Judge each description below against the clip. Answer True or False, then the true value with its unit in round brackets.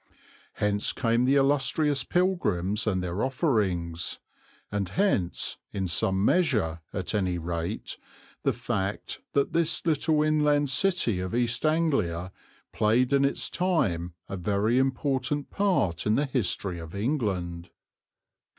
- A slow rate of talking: True (125 wpm)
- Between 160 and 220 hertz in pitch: False (115 Hz)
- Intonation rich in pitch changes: True (7.9 semitones)